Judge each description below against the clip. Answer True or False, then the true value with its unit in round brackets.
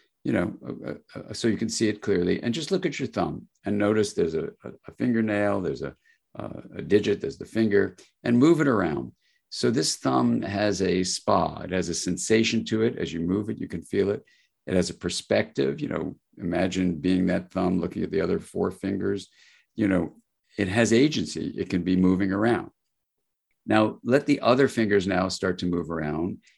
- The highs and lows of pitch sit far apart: False (3.4 semitones)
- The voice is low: True (100 Hz)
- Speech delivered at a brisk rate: True (210 wpm)